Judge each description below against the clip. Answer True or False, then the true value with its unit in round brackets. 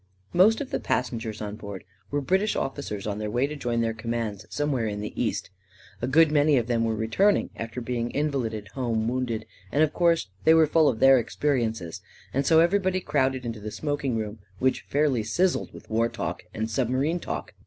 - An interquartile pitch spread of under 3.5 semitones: False (4.9 semitones)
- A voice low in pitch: True (125 Hz)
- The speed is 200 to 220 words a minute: True (205 wpm)